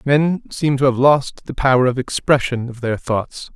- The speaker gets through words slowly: No, fast, 205 wpm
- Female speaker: No, male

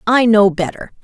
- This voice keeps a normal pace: Yes, average, 175 wpm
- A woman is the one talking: Yes, female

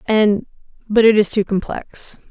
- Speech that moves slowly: Yes, slow, 130 wpm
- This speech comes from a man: No, female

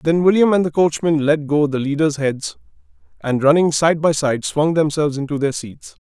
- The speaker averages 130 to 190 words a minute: No, average, 200 wpm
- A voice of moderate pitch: Yes, medium, 150 Hz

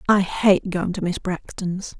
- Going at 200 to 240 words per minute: No, average, 180 wpm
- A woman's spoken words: Yes, female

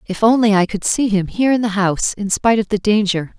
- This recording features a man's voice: No, female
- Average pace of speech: No, fast, 265 wpm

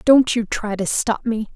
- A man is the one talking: No, female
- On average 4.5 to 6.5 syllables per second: No, 4.3 syllables/s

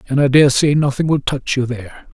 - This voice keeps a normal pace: No, fast, 245 wpm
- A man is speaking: Yes, male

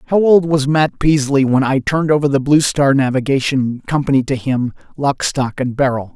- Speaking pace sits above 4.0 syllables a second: Yes, 5.1 syllables/s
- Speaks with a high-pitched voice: No, medium, 140 Hz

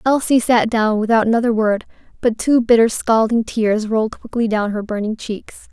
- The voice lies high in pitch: Yes, high, 225 Hz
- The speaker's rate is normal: Yes, average, 180 wpm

